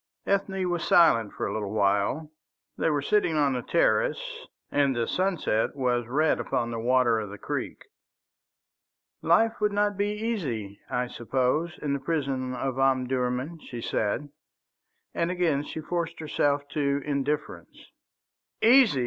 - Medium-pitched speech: Yes, medium, 145 Hz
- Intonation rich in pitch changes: Yes, wide, 5.8 semitones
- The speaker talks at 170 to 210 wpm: No, average, 145 wpm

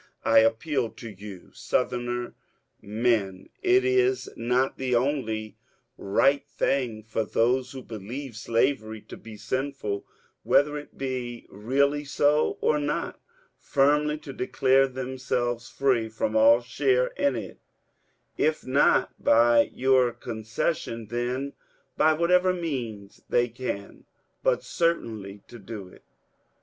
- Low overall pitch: Yes, low, 125 Hz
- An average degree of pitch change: Yes, average, 3.9 semitones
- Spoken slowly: Yes, slow, 120 wpm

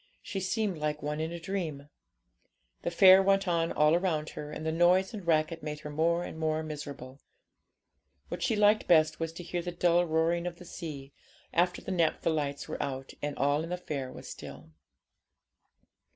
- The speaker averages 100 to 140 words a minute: No, average, 190 wpm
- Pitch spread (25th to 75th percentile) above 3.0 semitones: No, average, 2.7 semitones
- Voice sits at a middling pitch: Yes, medium, 165 Hz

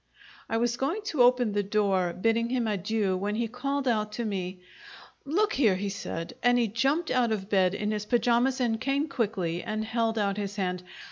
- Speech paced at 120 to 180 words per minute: No, average, 200 wpm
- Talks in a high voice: Yes, high, 225 Hz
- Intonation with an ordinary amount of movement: Yes, average, 3.5 semitones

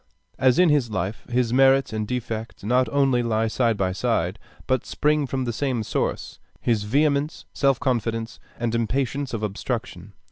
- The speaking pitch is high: No, low, 120 Hz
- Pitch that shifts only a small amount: No, average, 3.4 semitones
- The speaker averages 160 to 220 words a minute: Yes, average, 165 wpm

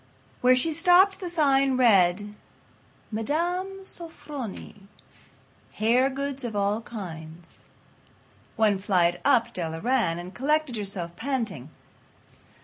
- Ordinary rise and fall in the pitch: No, wide, 6.7 semitones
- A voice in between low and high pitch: No, high, 230 Hz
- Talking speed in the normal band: No, slow, 105 wpm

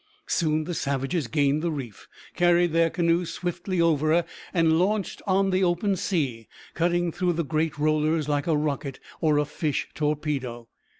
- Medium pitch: Yes, medium, 160 Hz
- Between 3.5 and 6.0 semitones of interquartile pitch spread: No, average, 2.8 semitones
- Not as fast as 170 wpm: Yes, average, 160 wpm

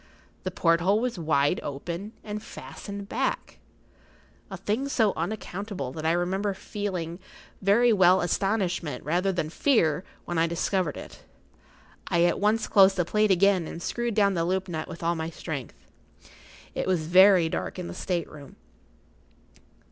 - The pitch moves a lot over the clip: No, average, 3.4 semitones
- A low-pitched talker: No, medium, 185 Hz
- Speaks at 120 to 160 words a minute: Yes, average, 150 wpm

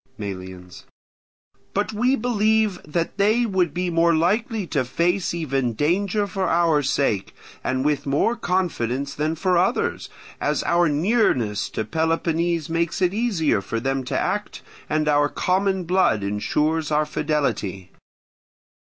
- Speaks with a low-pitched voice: No, medium, 165 Hz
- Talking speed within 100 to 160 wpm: Yes, slow, 135 wpm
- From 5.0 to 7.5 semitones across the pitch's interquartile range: Yes, wide, 5.4 semitones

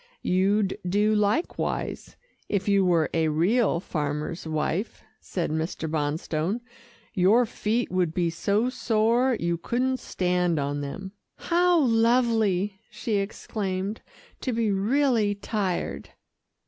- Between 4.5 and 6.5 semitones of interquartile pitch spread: Yes, average, 4.9 semitones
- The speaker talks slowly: Yes, slow, 115 wpm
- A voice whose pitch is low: No, high, 200 Hz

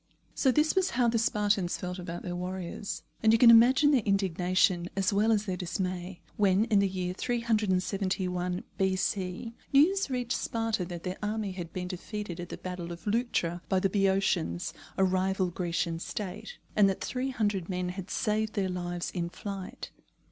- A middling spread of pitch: Yes, average, 3.2 semitones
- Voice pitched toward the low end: No, high, 190 Hz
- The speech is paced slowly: No, average, 175 wpm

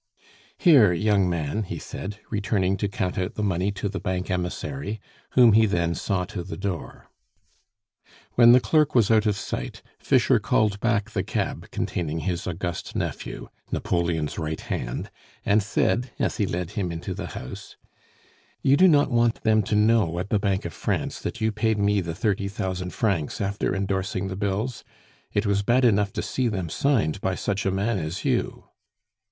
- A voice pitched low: Yes, low, 100 Hz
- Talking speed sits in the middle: Yes, average, 180 wpm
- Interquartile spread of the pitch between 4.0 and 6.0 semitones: No, average, 3.2 semitones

